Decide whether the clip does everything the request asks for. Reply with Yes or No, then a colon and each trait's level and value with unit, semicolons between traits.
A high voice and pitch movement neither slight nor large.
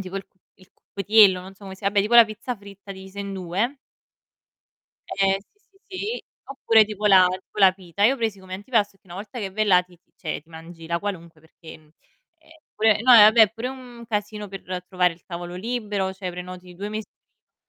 Yes: high, 200 Hz; average, 3.0 semitones